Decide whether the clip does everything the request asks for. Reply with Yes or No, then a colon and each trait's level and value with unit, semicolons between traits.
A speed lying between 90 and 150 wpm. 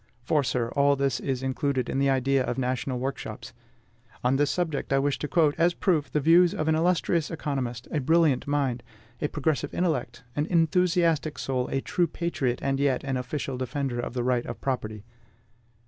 No: average, 185 wpm